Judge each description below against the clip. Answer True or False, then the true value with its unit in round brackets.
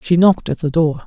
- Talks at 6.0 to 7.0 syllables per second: True (6.4 syllables/s)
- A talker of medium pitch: True (165 Hz)